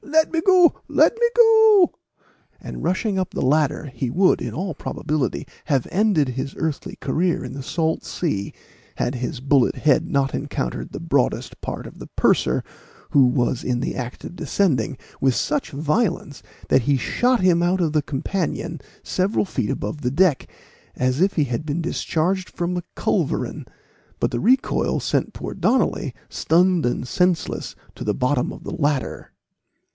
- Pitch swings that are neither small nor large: No, wide, 5.8 semitones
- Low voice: No, medium, 155 Hz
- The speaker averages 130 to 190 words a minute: Yes, average, 170 wpm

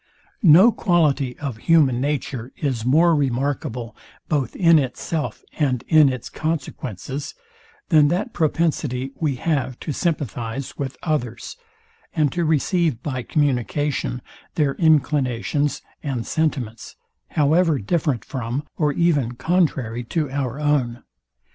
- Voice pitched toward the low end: No, medium, 145 Hz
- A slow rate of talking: Yes, slow, 115 wpm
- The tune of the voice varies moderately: Yes, average, 3.9 semitones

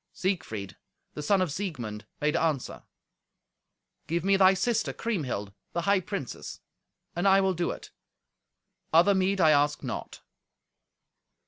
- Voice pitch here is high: No, medium, 175 Hz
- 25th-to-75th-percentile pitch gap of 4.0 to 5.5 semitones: Yes, average, 4.7 semitones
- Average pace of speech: No, slow, 130 wpm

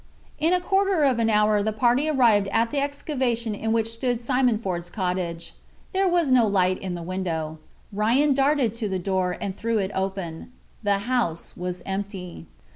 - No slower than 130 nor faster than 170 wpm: No, average, 180 wpm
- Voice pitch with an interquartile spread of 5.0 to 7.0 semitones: Yes, average, 5.3 semitones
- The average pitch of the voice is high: Yes, high, 215 Hz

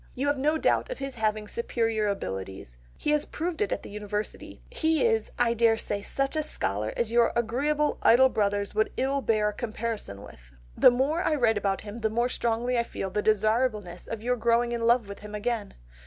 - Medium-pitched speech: No, high, 230 Hz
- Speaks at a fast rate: Yes, fast, 210 wpm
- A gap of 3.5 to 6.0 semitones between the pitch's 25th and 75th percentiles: Yes, average, 3.8 semitones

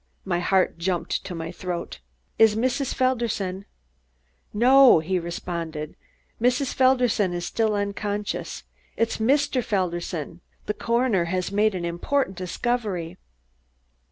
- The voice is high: Yes, high, 195 Hz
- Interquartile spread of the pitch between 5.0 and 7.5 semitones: Yes, wide, 5.5 semitones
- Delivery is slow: Yes, slow, 125 wpm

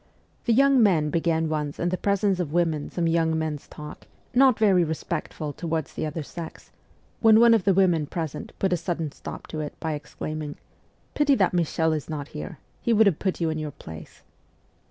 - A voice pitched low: No, medium, 165 Hz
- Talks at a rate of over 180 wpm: Yes, average, 200 wpm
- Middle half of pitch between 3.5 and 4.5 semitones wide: Yes, average, 3.9 semitones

